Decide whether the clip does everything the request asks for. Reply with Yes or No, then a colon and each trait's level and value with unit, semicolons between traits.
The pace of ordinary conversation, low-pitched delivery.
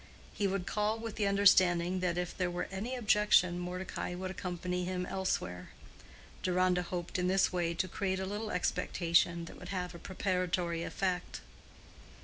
No: average, 160 wpm; medium, 180 Hz